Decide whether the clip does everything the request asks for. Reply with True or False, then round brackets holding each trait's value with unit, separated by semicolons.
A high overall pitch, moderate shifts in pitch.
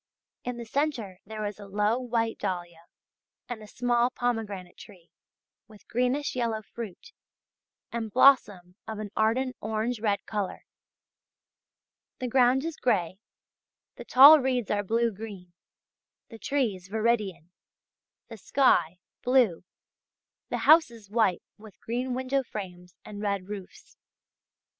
True (220 Hz; 3.7 semitones)